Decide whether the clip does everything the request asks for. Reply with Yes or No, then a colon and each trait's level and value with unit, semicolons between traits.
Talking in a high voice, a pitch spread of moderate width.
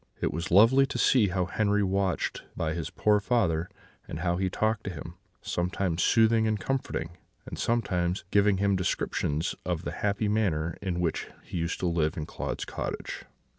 No: very low, 95 Hz; average, 3.4 semitones